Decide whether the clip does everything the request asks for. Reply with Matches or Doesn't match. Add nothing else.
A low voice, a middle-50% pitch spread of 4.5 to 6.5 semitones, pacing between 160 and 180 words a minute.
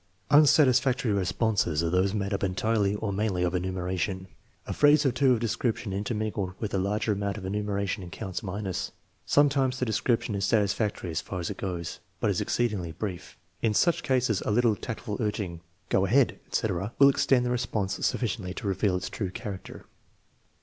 Doesn't match